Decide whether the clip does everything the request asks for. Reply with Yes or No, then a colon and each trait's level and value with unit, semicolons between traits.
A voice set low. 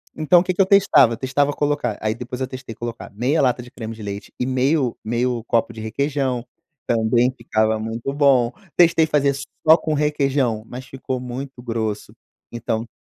Yes: low, 125 Hz